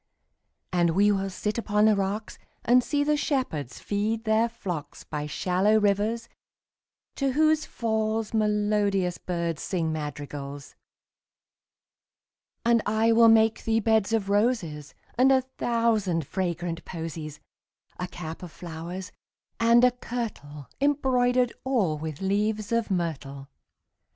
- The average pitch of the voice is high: Yes, high, 205 Hz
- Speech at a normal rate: No, slow, 130 wpm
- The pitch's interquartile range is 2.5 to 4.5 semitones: No, average, 5.3 semitones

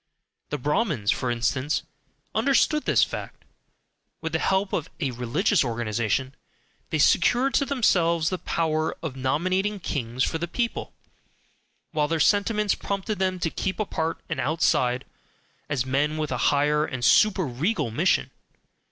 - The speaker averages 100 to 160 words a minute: Yes, average, 145 wpm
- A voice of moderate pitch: Yes, medium, 155 Hz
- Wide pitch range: Yes, wide, 6.5 semitones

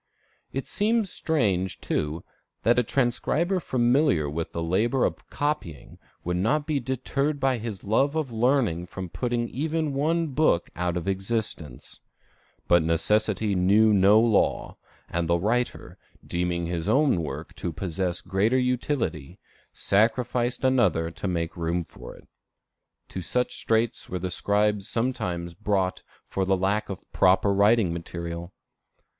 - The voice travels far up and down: Yes, wide, 6.4 semitones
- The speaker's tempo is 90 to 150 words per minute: Yes, average, 140 wpm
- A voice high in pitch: No, low, 105 Hz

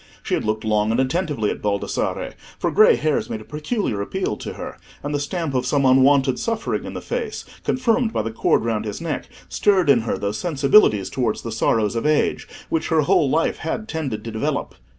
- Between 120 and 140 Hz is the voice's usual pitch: Yes, low, 135 Hz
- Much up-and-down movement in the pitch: Yes, wide, 6.9 semitones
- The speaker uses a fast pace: Yes, fast, 210 wpm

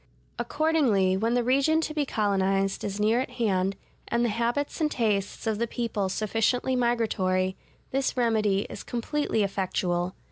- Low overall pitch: No, high, 225 Hz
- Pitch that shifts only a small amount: No, average, 4.2 semitones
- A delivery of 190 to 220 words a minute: No, average, 150 wpm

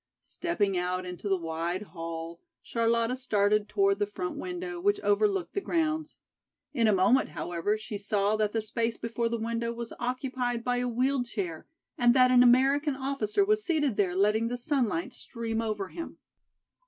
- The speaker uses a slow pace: No, average, 170 wpm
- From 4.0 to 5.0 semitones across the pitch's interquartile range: Yes, average, 4.5 semitones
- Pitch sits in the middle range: No, high, 230 Hz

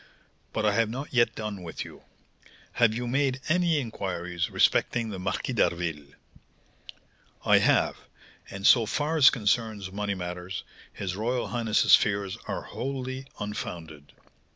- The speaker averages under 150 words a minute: Yes, average, 140 wpm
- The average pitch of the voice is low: Yes, low, 105 Hz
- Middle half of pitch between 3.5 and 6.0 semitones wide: Yes, average, 4.8 semitones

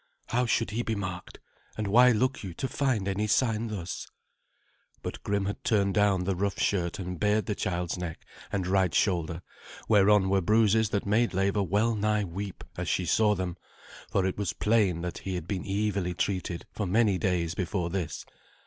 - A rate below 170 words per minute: No, average, 185 wpm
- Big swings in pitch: No, average, 2.8 semitones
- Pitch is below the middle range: Yes, low, 100 Hz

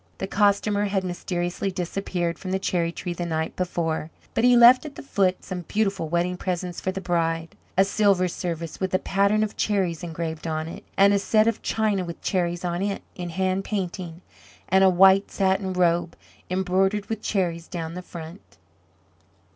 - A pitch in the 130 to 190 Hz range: Yes, medium, 185 Hz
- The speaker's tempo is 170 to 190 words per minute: Yes, average, 180 wpm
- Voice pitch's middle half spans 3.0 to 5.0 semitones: No, narrow, 2.4 semitones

